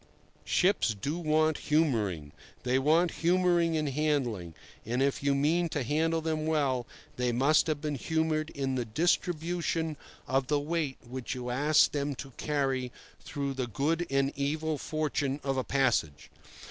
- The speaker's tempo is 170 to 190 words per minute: No, average, 155 wpm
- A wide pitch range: No, average, 3.2 semitones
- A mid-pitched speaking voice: Yes, medium, 145 Hz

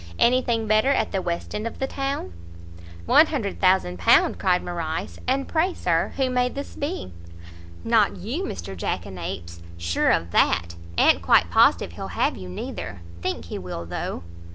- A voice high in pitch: No, medium, 180 Hz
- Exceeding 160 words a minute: No, average, 155 wpm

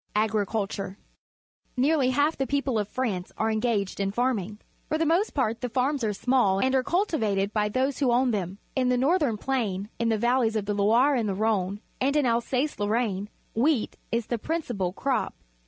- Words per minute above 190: Yes, fast, 205 wpm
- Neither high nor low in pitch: No, high, 235 Hz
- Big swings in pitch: No, average, 4.2 semitones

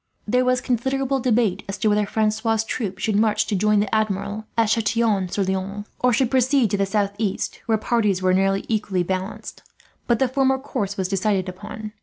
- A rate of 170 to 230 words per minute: Yes, average, 190 wpm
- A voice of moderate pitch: No, high, 215 Hz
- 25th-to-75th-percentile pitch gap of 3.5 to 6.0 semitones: No, average, 3.1 semitones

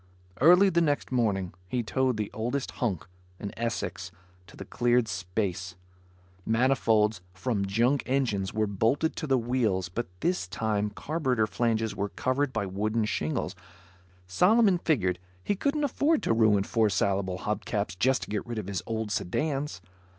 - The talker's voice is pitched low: Yes, low, 110 Hz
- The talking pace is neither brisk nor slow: Yes, average, 160 wpm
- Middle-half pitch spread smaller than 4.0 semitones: No, average, 5.0 semitones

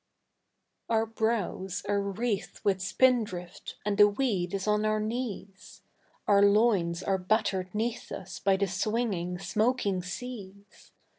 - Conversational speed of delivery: No, slow, 130 wpm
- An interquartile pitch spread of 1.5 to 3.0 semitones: Yes, average, 2.7 semitones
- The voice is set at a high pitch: Yes, high, 200 Hz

